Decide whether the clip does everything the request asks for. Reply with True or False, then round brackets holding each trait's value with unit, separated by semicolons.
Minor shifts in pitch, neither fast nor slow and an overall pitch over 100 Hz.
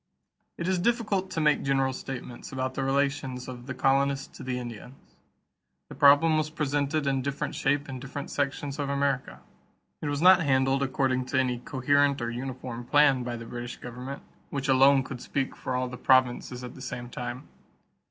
True (2.0 semitones; 185 wpm; 135 Hz)